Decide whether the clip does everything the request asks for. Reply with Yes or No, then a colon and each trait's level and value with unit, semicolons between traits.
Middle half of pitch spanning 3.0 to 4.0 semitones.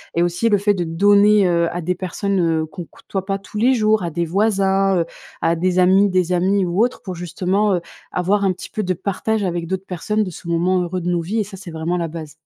No: narrow, 2.6 semitones